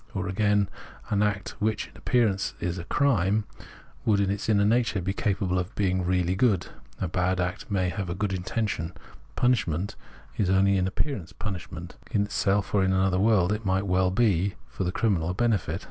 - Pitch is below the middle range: Yes, very low, 95 Hz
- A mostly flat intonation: Yes, narrow, 2.3 semitones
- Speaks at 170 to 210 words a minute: Yes, average, 190 wpm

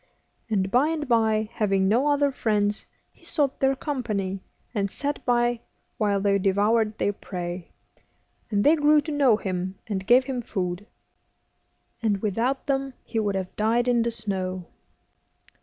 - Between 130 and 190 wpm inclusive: Yes, average, 155 wpm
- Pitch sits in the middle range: No, high, 220 Hz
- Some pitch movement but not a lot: Yes, average, 4.6 semitones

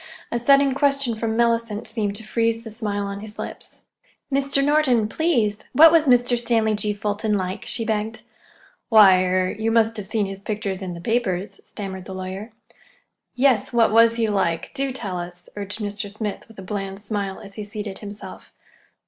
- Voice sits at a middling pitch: No, high, 215 Hz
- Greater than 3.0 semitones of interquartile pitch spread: No, average, 2.7 semitones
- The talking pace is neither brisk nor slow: Yes, average, 175 wpm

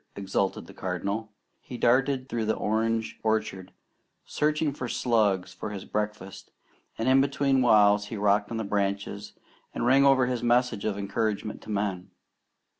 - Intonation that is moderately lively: Yes, average, 3.5 semitones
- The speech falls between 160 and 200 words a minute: No, average, 150 wpm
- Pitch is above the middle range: No, low, 110 Hz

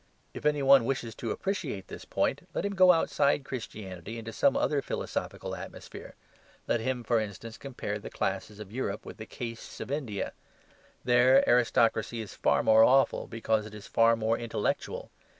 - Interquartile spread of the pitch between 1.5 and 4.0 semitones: Yes, average, 3.5 semitones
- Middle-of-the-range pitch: No, low, 115 Hz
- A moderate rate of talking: Yes, average, 170 wpm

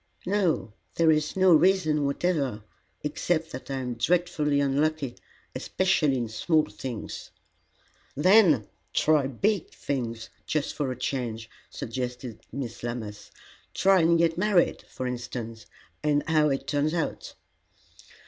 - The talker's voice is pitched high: No, medium, 145 Hz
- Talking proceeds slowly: Yes, slow, 130 wpm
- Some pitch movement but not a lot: Yes, average, 5.0 semitones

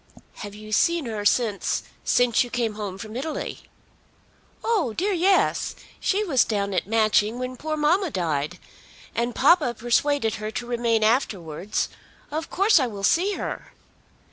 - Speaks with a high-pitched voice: Yes, high, 235 Hz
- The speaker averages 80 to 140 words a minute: No, average, 150 wpm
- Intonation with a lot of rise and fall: Yes, wide, 6.5 semitones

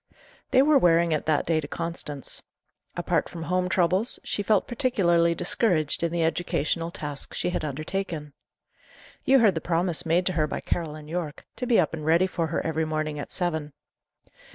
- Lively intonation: No, average, 2.8 semitones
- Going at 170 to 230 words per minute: Yes, average, 180 wpm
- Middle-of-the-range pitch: Yes, medium, 170 Hz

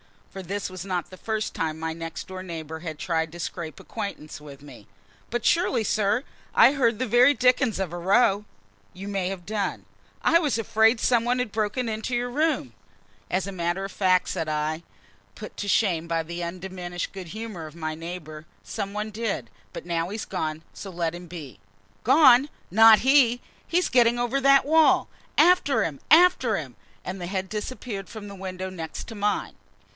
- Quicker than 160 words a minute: Yes, average, 185 wpm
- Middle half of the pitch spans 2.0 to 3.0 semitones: No, wide, 5.4 semitones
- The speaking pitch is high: Yes, high, 195 Hz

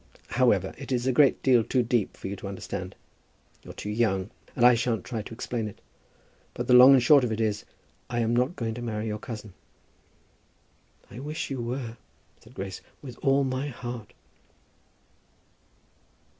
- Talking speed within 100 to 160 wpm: No, average, 180 wpm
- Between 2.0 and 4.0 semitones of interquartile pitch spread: Yes, average, 2.9 semitones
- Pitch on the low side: Yes, low, 120 Hz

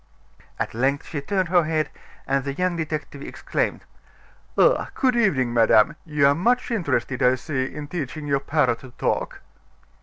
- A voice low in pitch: No, medium, 145 Hz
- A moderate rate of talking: Yes, average, 160 wpm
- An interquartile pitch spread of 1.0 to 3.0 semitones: No, average, 4.3 semitones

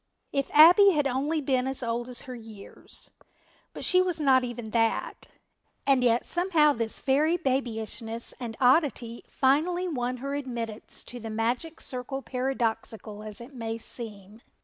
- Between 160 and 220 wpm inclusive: No, average, 150 wpm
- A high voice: Yes, very high, 250 Hz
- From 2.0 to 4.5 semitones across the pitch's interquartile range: Yes, average, 3.7 semitones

